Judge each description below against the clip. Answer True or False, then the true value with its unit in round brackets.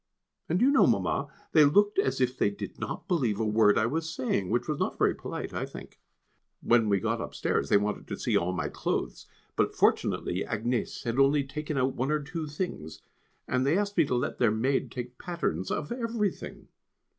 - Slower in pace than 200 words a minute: False (205 wpm)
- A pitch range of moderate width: False (6.4 semitones)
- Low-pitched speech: True (130 Hz)